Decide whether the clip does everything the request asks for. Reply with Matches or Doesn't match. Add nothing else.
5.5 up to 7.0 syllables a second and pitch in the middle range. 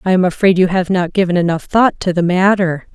Matches